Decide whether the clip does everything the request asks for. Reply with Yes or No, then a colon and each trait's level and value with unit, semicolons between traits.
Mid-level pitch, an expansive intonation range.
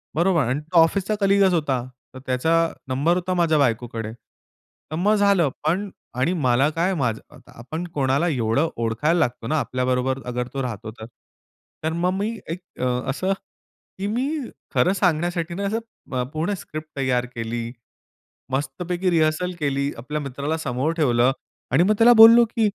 Yes: medium, 155 Hz; wide, 6.1 semitones